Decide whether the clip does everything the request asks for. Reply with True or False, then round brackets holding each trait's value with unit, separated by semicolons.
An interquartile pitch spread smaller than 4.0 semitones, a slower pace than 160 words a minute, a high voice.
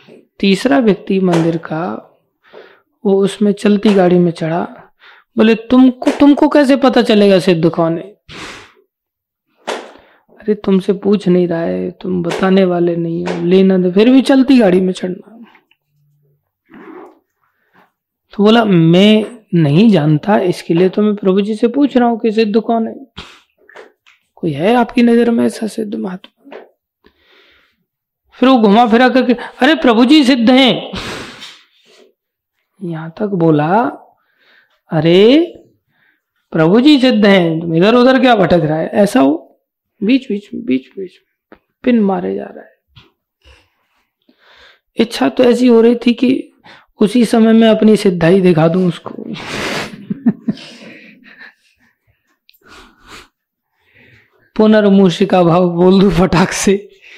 False (5.0 semitones; 130 wpm; 210 Hz)